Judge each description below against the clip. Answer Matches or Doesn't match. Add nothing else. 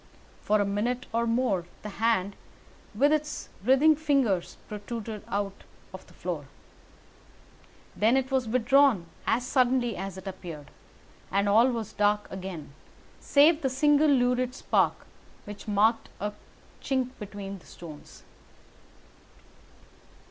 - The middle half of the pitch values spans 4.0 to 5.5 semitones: Matches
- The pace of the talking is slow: Matches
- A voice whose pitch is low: Doesn't match